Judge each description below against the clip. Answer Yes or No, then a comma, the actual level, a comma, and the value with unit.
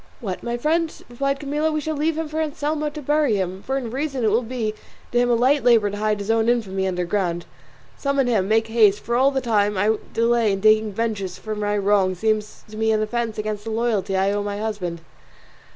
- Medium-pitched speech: No, high, 220 Hz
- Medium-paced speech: No, fast, 230 wpm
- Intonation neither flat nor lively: Yes, average, 4.0 semitones